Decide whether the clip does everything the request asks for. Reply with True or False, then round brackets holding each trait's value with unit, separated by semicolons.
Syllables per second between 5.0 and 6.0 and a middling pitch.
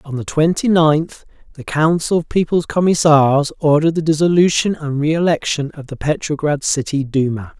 True (5.1 syllables/s; 155 Hz)